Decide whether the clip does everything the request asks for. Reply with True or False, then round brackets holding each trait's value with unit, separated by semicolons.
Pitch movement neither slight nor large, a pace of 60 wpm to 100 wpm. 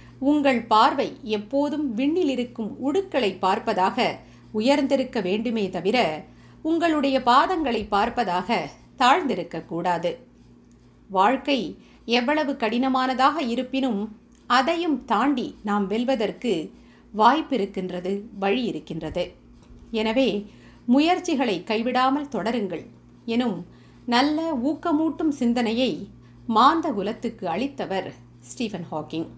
False (5.8 semitones; 75 wpm)